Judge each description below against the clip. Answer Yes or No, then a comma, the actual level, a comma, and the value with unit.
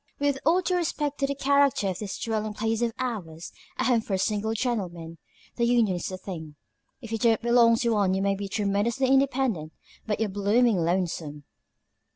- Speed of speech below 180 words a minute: No, average, 190 wpm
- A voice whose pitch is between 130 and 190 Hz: No, high, 220 Hz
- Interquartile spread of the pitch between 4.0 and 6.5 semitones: Yes, average, 4.4 semitones